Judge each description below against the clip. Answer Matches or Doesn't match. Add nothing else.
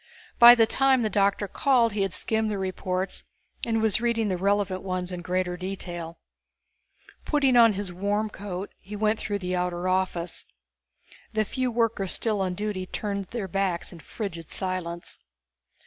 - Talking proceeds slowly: Doesn't match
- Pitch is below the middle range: Doesn't match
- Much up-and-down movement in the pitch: Doesn't match